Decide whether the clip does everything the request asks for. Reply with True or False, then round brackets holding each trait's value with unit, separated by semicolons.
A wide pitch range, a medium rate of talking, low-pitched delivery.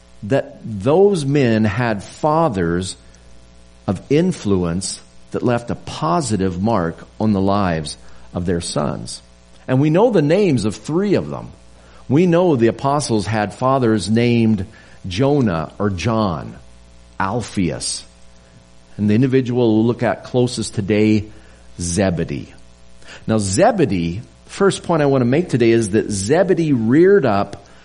False (7.6 semitones; 130 wpm; 105 Hz)